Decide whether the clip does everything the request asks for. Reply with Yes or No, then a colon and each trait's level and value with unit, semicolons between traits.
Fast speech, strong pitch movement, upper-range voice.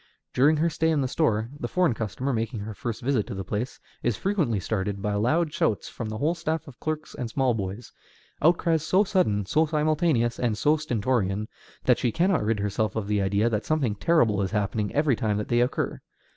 No: fast, 210 wpm; wide, 6.7 semitones; low, 120 Hz